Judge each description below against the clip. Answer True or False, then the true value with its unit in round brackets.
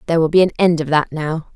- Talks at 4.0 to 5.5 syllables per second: False (7.1 syllables/s)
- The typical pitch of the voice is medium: True (160 Hz)